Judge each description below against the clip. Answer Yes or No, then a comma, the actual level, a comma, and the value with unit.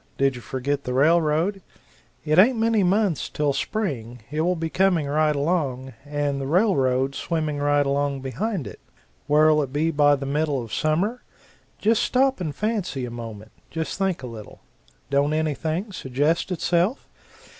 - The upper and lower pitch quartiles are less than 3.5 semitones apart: No, average, 4.6 semitones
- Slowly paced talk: No, average, 160 wpm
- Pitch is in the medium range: Yes, medium, 150 Hz